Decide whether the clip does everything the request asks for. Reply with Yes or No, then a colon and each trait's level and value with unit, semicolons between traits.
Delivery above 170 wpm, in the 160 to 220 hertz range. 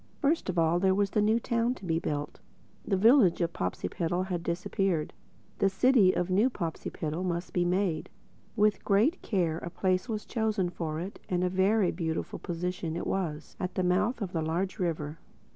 Yes: average, 180 wpm; medium, 185 Hz